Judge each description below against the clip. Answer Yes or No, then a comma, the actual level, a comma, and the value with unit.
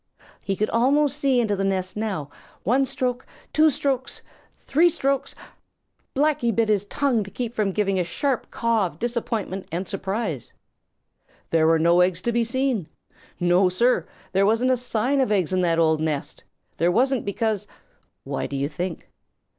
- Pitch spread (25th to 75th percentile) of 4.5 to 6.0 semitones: Yes, wide, 5.5 semitones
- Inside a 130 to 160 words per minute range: No, average, 170 wpm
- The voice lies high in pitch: Yes, high, 215 Hz